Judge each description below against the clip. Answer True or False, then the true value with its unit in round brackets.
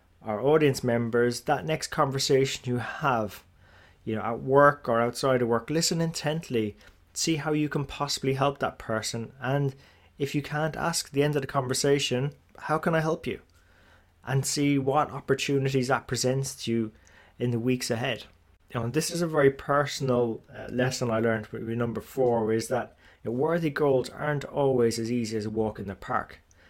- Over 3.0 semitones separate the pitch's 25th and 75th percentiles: True (4.2 semitones)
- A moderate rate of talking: True (190 wpm)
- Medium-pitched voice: False (130 Hz)